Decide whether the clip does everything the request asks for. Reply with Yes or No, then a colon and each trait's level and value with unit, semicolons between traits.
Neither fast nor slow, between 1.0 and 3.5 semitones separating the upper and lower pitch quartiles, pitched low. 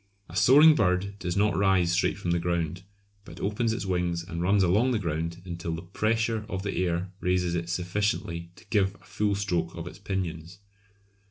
Yes: average, 190 wpm; average, 2.9 semitones; very low, 90 Hz